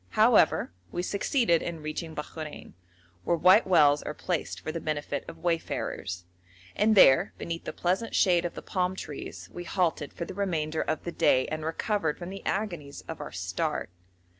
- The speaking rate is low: No, average, 175 wpm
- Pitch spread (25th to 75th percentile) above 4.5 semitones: No, average, 3.3 semitones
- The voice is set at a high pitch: No, medium, 165 Hz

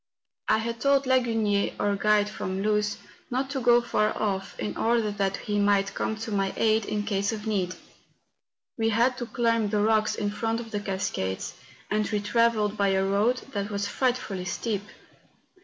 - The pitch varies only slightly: Yes, narrow, 2.3 semitones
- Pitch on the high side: Yes, high, 210 Hz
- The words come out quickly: No, average, 180 wpm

